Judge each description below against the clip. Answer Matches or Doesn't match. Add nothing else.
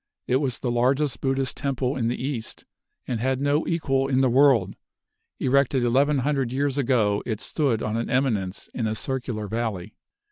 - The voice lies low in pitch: Matches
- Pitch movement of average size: Matches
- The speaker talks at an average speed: Matches